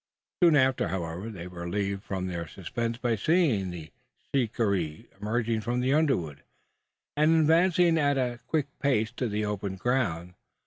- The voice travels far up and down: Yes, wide, 6.4 semitones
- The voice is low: Yes, low, 115 Hz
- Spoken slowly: No, average, 150 wpm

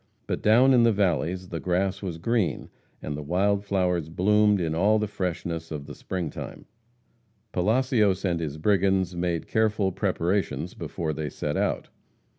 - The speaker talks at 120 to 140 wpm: No, average, 160 wpm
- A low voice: Yes, very low, 95 Hz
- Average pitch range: Yes, average, 3.7 semitones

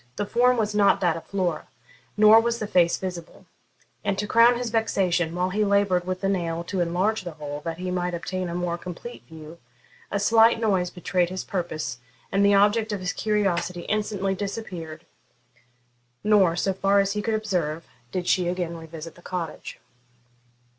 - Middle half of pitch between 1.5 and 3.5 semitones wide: Yes, average, 3.2 semitones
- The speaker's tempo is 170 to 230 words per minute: Yes, average, 180 wpm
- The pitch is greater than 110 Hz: Yes, medium, 185 Hz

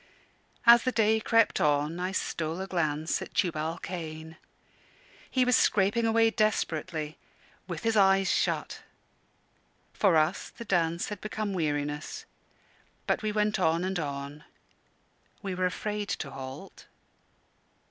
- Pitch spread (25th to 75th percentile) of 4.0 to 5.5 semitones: Yes, average, 5.2 semitones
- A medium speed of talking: No, slow, 130 wpm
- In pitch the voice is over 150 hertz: Yes, medium, 185 Hz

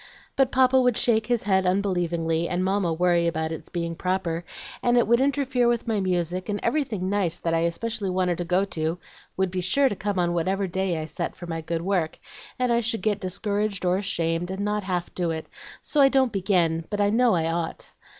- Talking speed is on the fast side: Yes, fast, 220 wpm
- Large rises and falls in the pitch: No, average, 3.9 semitones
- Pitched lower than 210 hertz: Yes, medium, 185 Hz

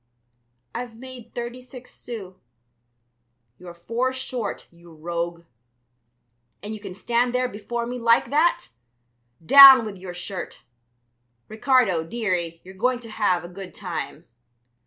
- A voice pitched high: Yes, high, 220 Hz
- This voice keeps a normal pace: No, slow, 130 wpm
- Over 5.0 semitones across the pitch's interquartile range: Yes, wide, 5.5 semitones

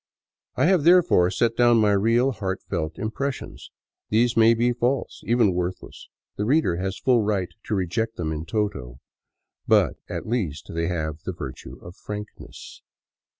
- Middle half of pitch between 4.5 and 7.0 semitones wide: Yes, average, 5.3 semitones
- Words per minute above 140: Yes, average, 150 wpm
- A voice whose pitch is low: Yes, low, 105 Hz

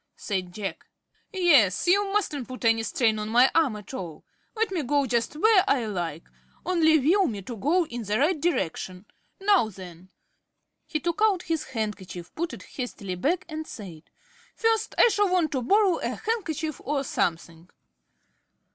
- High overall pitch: Yes, very high, 275 Hz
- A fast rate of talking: No, average, 165 wpm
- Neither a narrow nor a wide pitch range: No, wide, 8.9 semitones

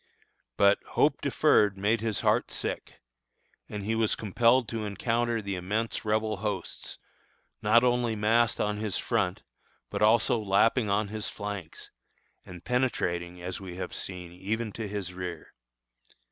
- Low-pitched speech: Yes, low, 105 Hz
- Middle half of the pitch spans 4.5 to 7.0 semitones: No, average, 2.9 semitones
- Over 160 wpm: No, average, 145 wpm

